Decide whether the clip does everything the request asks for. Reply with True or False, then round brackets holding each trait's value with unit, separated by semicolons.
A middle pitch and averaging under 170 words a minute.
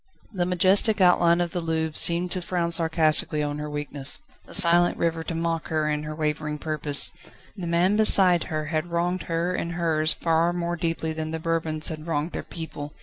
False (165 Hz; 195 wpm)